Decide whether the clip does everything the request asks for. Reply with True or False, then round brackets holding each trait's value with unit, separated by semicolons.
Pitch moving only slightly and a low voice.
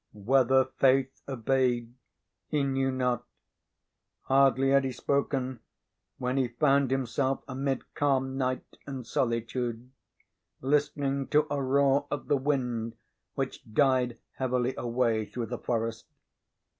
True (1.8 semitones; 130 Hz)